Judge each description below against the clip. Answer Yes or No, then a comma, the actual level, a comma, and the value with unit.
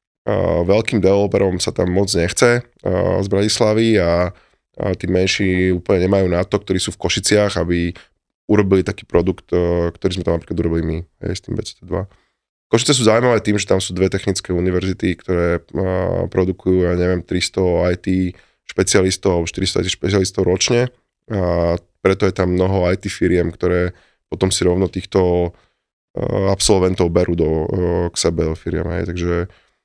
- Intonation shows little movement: Yes, narrow, 1.9 semitones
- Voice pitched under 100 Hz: Yes, very low, 90 Hz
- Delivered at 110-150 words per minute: No, average, 160 wpm